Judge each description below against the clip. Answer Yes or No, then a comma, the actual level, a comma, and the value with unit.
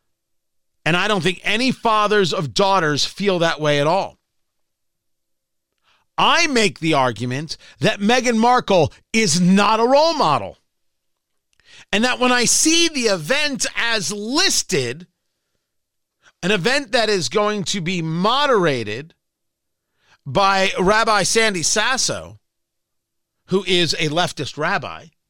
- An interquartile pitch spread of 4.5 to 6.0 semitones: Yes, average, 5.0 semitones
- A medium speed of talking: No, slow, 120 wpm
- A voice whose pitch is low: No, high, 200 Hz